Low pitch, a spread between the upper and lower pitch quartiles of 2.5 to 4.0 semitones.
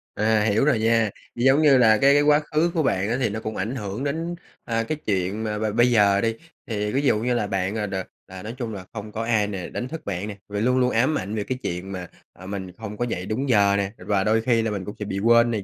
Yes: low, 110 Hz; average, 3.4 semitones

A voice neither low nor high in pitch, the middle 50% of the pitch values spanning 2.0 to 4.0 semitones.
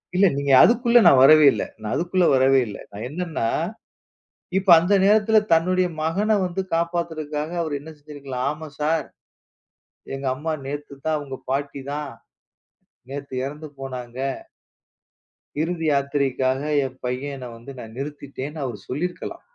Yes: medium, 145 Hz; average, 3.5 semitones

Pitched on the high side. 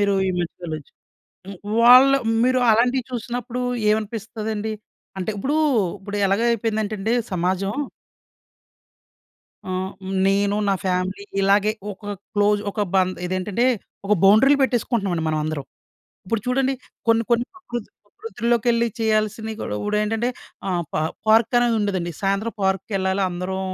Yes: high, 210 Hz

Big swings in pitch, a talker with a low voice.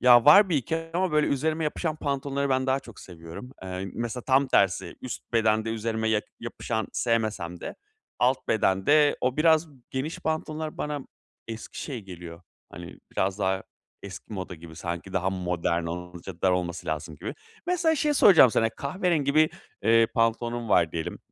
Yes: wide, 7.7 semitones; low, 115 Hz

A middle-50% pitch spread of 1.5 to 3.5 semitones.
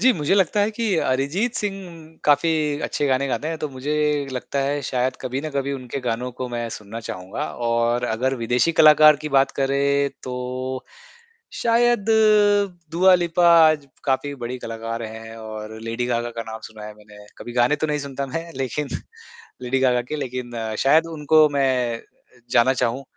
No: average, 4.1 semitones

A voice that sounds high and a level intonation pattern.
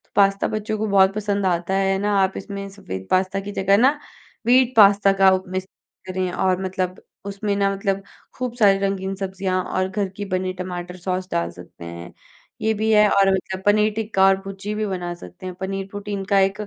Yes: high, 195 Hz; narrow, 1.6 semitones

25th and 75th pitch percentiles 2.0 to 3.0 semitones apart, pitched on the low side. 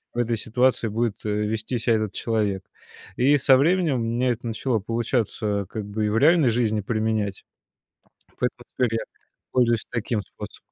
Yes: narrow, 2.5 semitones; low, 115 Hz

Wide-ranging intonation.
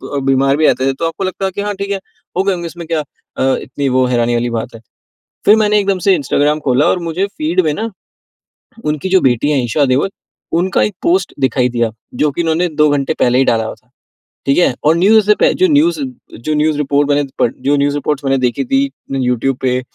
Yes: wide, 5.9 semitones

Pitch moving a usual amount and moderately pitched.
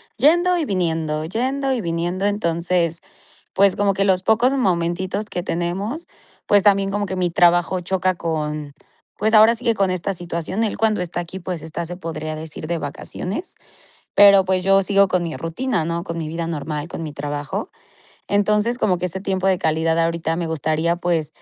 Yes: average, 3.4 semitones; medium, 180 Hz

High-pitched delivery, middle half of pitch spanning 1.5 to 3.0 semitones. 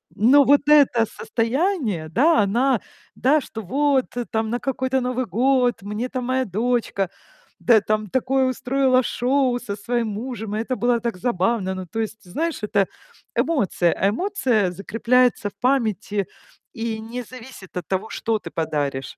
No: high, 235 Hz; average, 3.9 semitones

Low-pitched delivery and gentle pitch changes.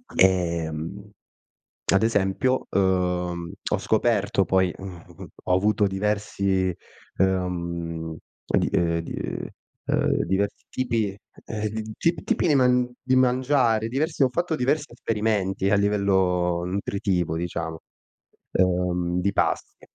No: very low, 95 Hz; average, 3.9 semitones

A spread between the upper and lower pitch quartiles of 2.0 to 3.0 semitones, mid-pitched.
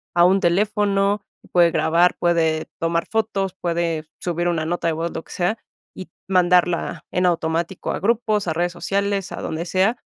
Yes: average, 2.7 semitones; medium, 175 Hz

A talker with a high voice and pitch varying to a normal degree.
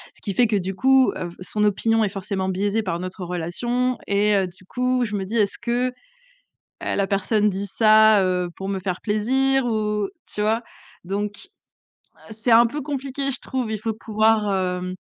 Yes: high, 210 Hz; average, 3.5 semitones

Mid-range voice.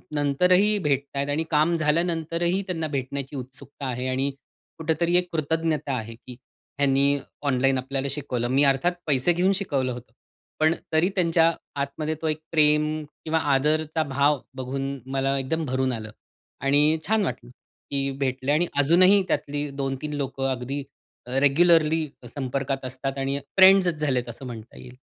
Yes: medium, 145 Hz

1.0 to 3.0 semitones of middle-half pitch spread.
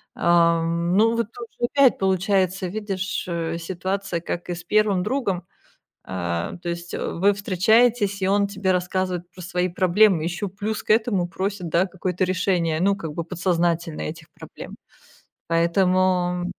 Yes: narrow, 2.5 semitones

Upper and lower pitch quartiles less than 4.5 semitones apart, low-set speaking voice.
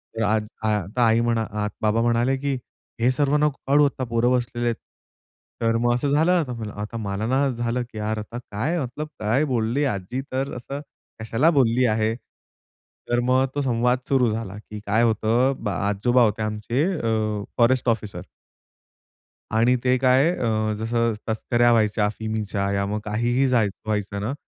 Yes: average, 2.9 semitones; low, 115 Hz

